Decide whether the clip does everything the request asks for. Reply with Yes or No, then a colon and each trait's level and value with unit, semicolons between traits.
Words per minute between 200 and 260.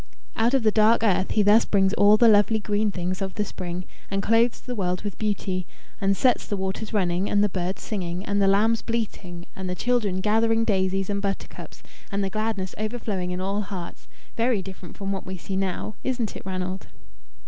Yes: fast, 205 wpm